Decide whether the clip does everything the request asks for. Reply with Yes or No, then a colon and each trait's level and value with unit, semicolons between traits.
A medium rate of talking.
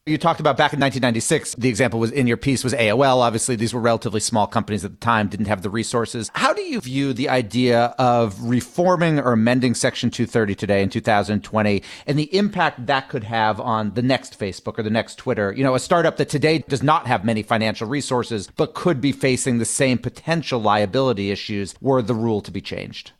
No: fast, 215 wpm